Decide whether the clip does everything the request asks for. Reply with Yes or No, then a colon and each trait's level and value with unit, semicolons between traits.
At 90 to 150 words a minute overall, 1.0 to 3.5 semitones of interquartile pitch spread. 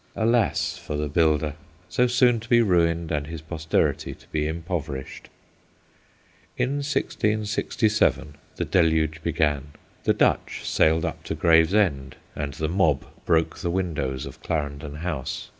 No: slow, 135 wpm; average, 4.1 semitones